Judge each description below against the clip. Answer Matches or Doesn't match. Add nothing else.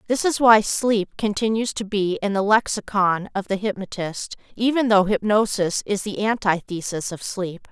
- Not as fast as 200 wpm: Matches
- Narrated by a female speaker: Matches